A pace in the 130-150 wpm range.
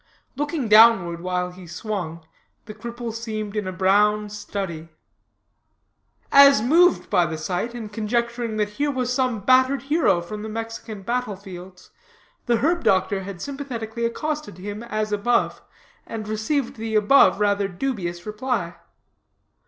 Yes: average, 140 wpm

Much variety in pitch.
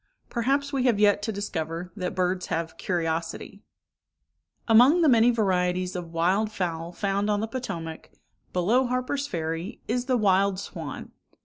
No: average, 4.9 semitones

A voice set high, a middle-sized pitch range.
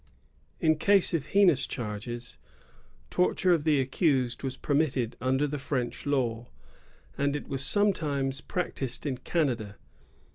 No: medium, 140 Hz; average, 3.8 semitones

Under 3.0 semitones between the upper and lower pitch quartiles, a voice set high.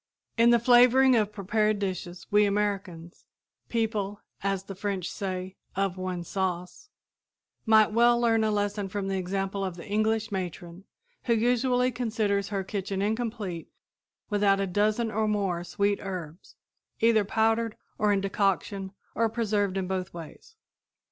Yes: narrow, 2.5 semitones; high, 205 Hz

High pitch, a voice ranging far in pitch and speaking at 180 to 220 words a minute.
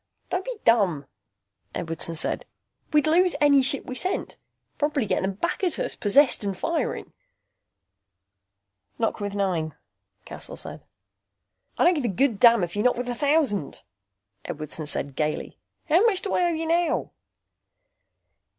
No: high, 245 Hz; wide, 8.7 semitones; average, 150 wpm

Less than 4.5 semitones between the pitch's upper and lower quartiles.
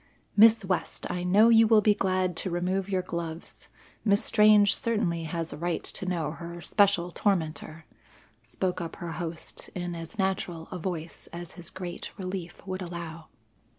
Yes: narrow, 2.5 semitones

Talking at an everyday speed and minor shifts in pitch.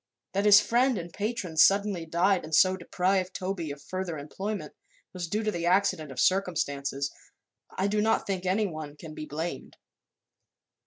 No: average, 160 wpm; average, 3.9 semitones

